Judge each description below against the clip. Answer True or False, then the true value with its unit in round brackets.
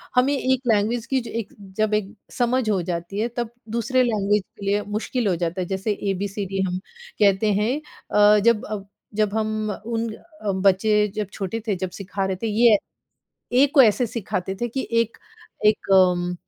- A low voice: False (210 Hz)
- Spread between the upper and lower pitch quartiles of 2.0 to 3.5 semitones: True (3.1 semitones)